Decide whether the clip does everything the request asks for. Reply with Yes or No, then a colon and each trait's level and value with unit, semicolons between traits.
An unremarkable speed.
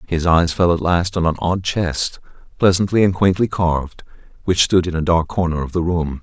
No: fast, 210 wpm